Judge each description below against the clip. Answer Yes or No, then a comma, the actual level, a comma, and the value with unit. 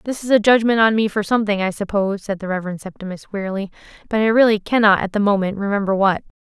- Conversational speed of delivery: No, fast, 225 wpm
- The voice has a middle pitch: No, high, 205 Hz